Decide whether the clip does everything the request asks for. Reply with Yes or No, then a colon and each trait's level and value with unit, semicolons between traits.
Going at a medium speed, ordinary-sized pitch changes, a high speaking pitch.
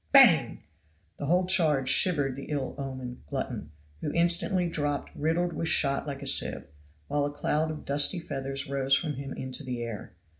No: average, 175 wpm; average, 3.0 semitones; medium, 145 Hz